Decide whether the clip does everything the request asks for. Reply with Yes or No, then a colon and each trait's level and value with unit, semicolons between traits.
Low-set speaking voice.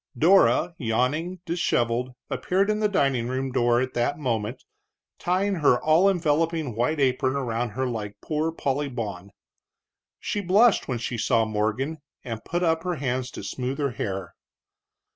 Yes: low, 130 Hz